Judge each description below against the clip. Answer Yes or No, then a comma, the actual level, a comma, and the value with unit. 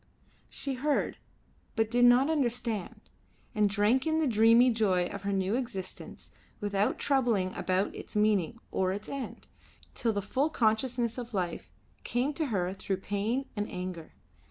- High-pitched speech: Yes, high, 220 Hz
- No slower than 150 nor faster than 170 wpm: Yes, average, 155 wpm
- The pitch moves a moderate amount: Yes, average, 3.9 semitones